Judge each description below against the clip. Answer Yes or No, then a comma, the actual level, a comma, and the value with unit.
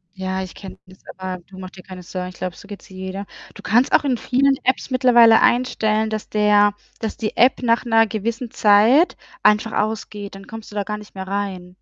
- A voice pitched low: No, high, 210 Hz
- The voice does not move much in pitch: No, average, 3.1 semitones